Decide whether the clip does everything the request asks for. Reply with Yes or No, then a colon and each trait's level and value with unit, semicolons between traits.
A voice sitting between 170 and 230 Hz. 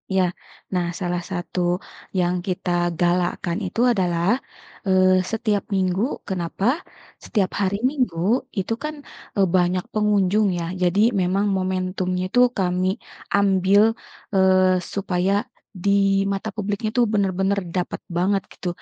Yes: medium, 185 Hz